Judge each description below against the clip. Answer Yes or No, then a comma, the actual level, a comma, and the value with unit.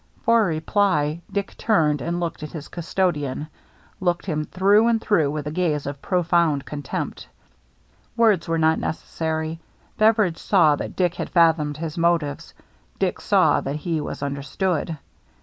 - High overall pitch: No, medium, 165 Hz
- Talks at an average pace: Yes, average, 150 wpm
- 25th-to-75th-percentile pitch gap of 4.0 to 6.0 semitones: No, average, 3.3 semitones